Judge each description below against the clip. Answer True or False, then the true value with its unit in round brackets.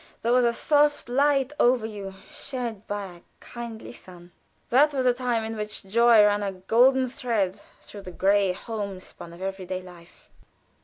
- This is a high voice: True (220 Hz)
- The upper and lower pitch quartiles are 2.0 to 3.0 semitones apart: False (4.3 semitones)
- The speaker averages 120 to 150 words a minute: False (170 wpm)